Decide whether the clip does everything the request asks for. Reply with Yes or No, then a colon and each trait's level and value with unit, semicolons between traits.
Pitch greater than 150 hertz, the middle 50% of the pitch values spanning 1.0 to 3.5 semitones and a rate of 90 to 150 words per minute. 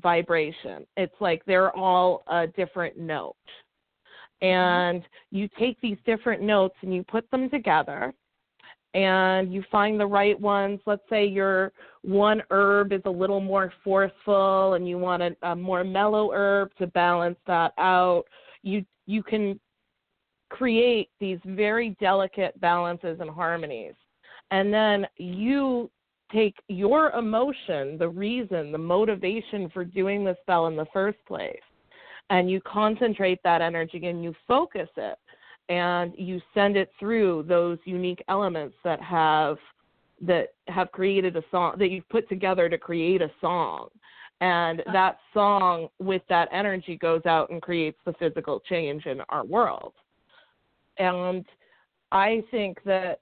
Yes: high, 190 Hz; average, 2.7 semitones; average, 145 wpm